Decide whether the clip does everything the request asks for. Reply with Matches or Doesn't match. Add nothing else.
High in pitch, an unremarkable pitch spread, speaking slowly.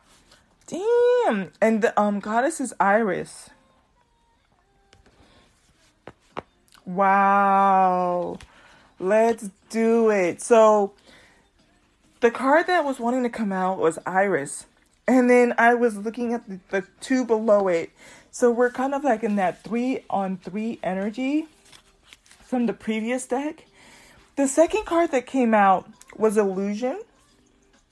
Matches